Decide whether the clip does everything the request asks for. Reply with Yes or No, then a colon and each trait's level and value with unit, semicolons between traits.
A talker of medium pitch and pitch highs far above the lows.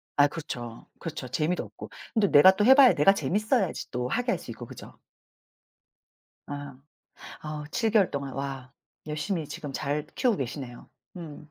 Yes: medium, 150 Hz; wide, 6.0 semitones